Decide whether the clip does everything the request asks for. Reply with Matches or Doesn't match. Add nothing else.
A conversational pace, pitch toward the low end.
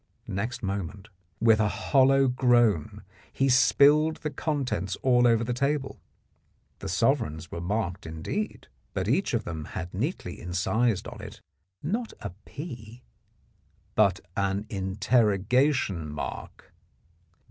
Doesn't match